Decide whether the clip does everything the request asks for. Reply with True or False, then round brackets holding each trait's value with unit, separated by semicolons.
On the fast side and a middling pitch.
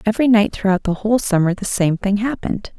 False (215 wpm; 205 Hz)